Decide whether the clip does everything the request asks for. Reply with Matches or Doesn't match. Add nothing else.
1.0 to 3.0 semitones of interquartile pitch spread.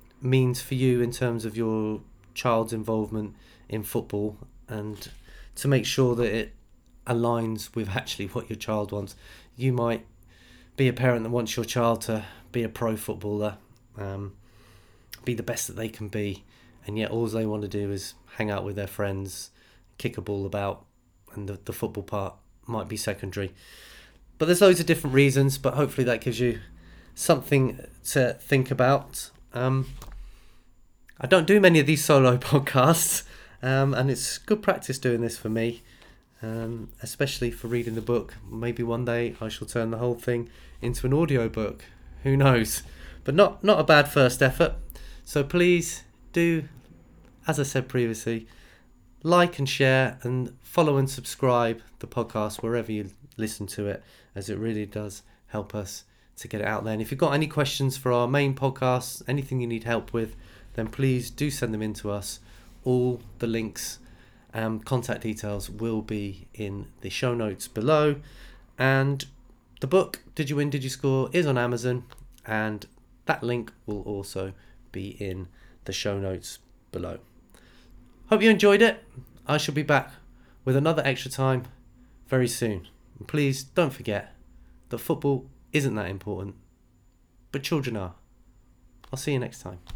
Doesn't match